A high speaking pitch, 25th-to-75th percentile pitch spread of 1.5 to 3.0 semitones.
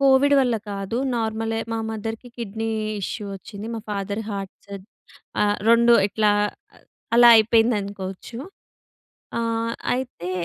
Yes: high, 225 Hz; narrow, 2.4 semitones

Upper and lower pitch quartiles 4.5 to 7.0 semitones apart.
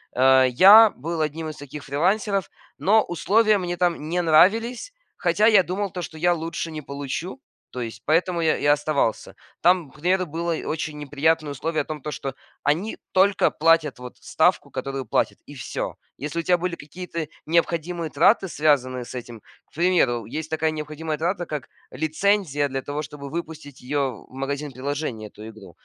No: average, 3.7 semitones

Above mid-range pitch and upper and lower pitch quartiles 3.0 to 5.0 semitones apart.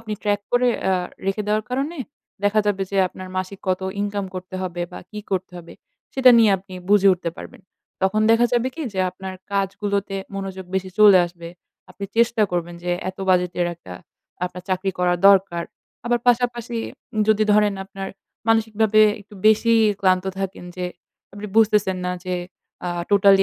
No: high, 200 Hz; narrow, 2.5 semitones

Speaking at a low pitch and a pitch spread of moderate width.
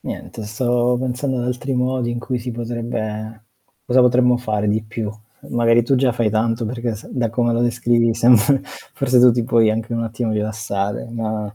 No: low, 120 Hz; narrow, 2.0 semitones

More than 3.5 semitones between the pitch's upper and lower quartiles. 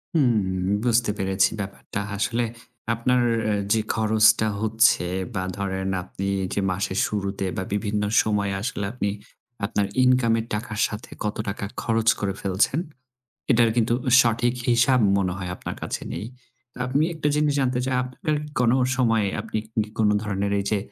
No: average, 3.2 semitones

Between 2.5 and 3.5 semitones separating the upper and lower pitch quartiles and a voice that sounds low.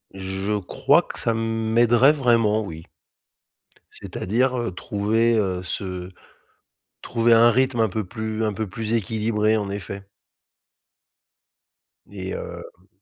Yes: average, 2.8 semitones; low, 110 Hz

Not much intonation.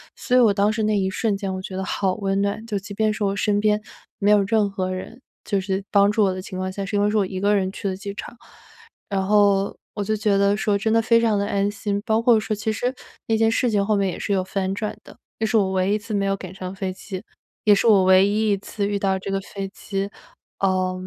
Yes: narrow, 1.6 semitones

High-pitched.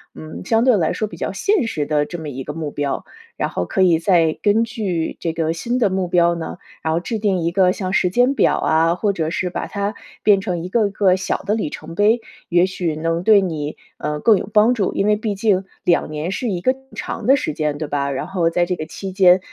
No: medium, 180 Hz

